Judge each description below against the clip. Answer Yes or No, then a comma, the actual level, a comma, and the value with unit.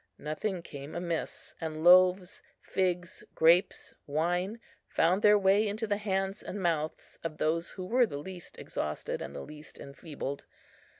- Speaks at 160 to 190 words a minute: No, average, 145 wpm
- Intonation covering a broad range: No, average, 3.6 semitones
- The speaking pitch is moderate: Yes, medium, 175 Hz